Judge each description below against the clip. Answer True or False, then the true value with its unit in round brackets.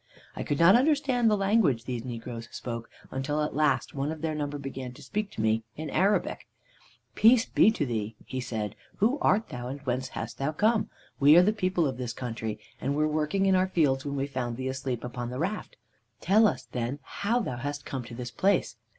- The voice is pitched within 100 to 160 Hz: True (140 Hz)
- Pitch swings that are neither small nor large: False (7.3 semitones)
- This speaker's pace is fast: True (215 wpm)